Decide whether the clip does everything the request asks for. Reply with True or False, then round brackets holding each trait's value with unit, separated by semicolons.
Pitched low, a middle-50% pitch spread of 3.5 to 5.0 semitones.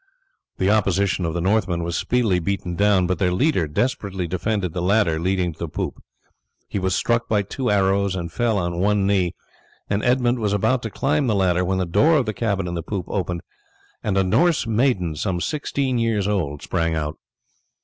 True (95 Hz; 3.9 semitones)